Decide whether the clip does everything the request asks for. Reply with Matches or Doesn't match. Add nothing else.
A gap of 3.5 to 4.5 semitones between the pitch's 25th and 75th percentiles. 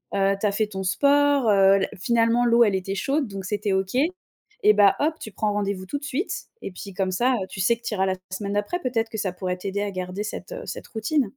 Matches